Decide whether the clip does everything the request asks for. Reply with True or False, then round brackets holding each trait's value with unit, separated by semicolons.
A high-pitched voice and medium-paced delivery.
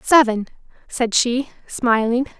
False (240 Hz; 100 wpm)